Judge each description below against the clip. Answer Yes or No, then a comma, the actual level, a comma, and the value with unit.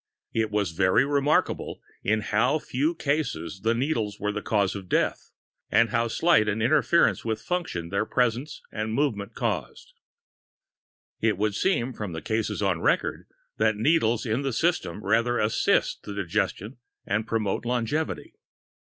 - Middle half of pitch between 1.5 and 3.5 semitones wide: No, average, 4.3 semitones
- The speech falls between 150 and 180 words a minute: Yes, average, 155 wpm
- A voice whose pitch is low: Yes, low, 110 Hz